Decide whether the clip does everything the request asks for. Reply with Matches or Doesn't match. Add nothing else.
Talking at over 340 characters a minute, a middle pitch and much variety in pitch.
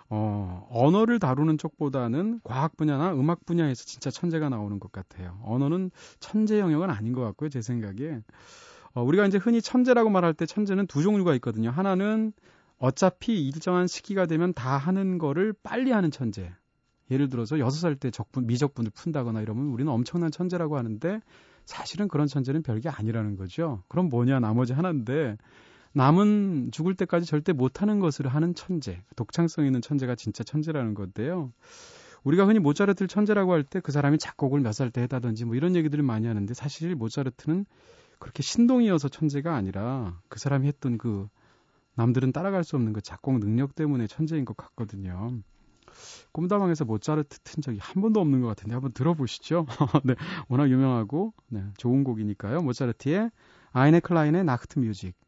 Matches